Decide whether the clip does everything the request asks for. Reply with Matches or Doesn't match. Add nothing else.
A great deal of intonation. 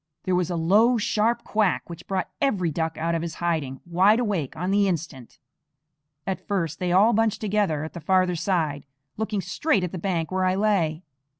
Doesn't match